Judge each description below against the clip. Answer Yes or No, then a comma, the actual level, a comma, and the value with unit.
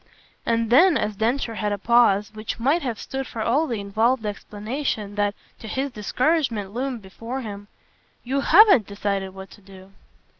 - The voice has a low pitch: No, high, 225 Hz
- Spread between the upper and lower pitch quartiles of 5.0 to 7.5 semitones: No, average, 4.3 semitones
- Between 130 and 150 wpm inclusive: No, average, 165 wpm